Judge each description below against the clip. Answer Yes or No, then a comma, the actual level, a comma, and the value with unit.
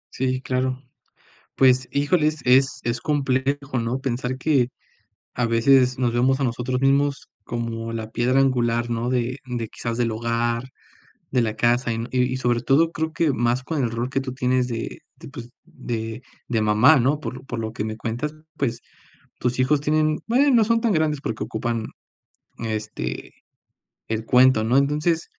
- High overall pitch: No, low, 125 Hz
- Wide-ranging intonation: No, average, 2.7 semitones